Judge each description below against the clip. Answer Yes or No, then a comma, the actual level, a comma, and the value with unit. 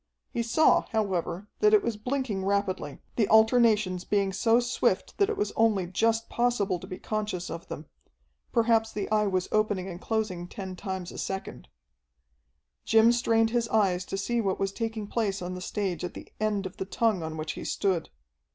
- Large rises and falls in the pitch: No, average, 3.4 semitones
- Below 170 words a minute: No, average, 190 wpm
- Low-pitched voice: No, high, 205 Hz